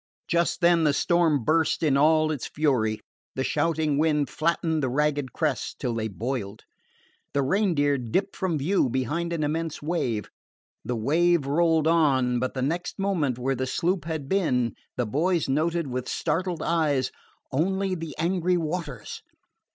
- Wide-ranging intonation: No, average, 4.3 semitones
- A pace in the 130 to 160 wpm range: Yes, average, 155 wpm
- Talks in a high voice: No, medium, 155 Hz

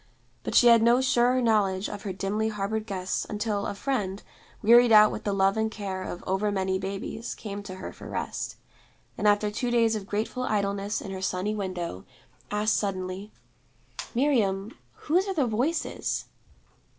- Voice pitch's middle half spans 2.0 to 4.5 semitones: Yes, average, 2.8 semitones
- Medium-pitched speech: No, high, 210 Hz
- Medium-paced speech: Yes, average, 170 wpm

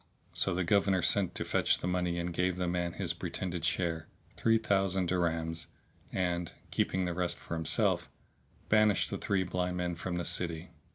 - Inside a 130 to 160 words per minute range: No, average, 175 wpm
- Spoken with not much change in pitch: Yes, narrow, 1.4 semitones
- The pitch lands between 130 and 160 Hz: No, very low, 90 Hz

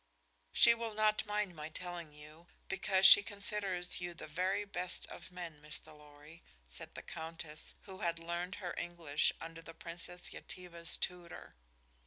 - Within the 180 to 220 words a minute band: No, average, 155 wpm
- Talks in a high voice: No, medium, 175 Hz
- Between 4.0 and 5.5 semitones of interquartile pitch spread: No, narrow, 2.6 semitones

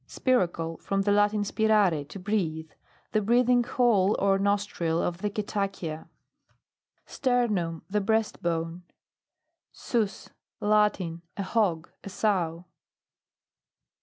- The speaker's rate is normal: No, slow, 105 wpm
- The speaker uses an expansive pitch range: No, average, 3.8 semitones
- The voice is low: No, high, 200 Hz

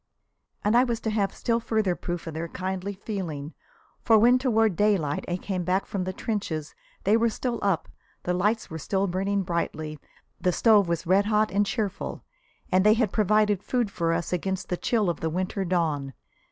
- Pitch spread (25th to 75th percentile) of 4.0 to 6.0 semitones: No, average, 3.6 semitones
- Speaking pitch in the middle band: No, high, 195 Hz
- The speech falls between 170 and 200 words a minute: Yes, average, 195 wpm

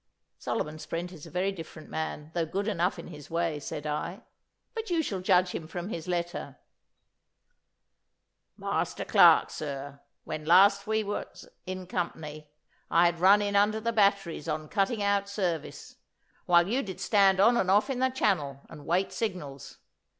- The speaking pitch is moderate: Yes, medium, 180 Hz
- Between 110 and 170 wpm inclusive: Yes, average, 165 wpm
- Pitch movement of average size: Yes, average, 4.2 semitones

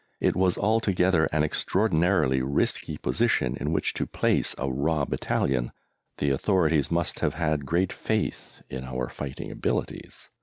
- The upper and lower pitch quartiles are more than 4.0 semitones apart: Yes, average, 4.9 semitones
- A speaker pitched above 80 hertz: No, very low, 75 Hz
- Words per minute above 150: No, average, 145 wpm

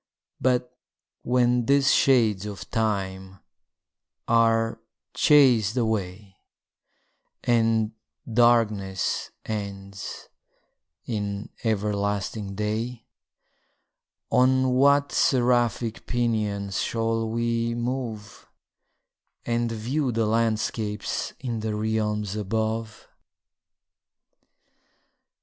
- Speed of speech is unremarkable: No, slow, 70 wpm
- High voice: No, low, 115 Hz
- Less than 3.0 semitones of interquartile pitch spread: Yes, narrow, 2.4 semitones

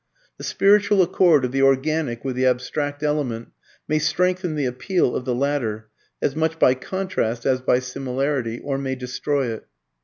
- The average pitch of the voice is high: No, low, 135 Hz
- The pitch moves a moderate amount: Yes, average, 3.6 semitones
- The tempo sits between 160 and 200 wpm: Yes, average, 165 wpm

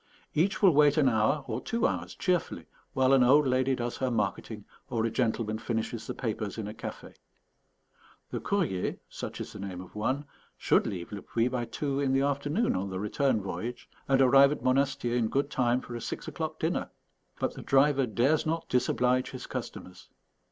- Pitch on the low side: Yes, low, 125 Hz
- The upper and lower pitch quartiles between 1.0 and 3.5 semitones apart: No, average, 4.0 semitones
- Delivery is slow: No, average, 190 wpm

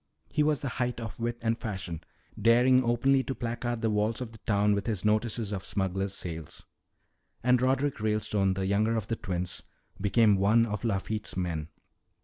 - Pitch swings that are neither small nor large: Yes, average, 3.3 semitones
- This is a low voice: Yes, low, 110 Hz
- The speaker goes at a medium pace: Yes, average, 175 wpm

